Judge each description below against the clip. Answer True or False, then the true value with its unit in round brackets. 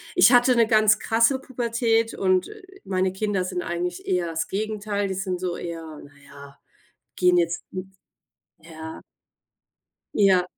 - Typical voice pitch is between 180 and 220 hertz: True (190 Hz)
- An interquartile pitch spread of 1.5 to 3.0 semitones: False (3.8 semitones)